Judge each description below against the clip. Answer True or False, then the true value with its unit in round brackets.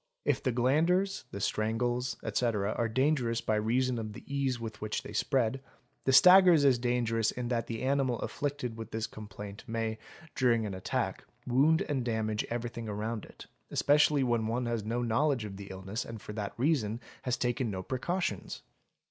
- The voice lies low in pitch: True (120 Hz)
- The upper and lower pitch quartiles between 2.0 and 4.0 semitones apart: True (3.2 semitones)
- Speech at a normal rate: True (175 wpm)